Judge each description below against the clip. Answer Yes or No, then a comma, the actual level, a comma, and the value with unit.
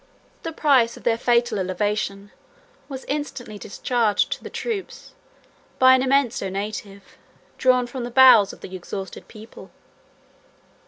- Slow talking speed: Yes, slow, 130 wpm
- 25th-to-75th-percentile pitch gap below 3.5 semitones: No, average, 4.2 semitones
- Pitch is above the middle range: Yes, high, 235 Hz